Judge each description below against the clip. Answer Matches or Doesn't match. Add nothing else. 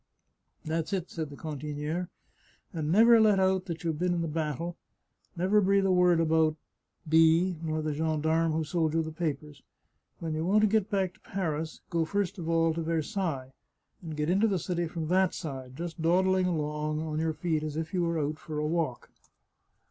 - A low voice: Doesn't match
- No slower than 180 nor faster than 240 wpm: Matches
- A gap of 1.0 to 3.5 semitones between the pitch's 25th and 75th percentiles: Matches